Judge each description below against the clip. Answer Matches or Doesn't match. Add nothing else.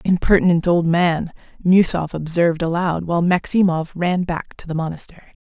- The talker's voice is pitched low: Doesn't match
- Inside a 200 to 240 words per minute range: Doesn't match